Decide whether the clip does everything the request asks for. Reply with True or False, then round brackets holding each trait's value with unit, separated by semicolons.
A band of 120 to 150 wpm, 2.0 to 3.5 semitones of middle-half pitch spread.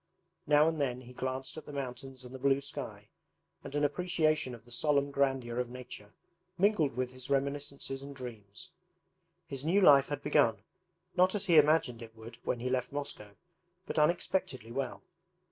False (175 wpm; 2.9 semitones)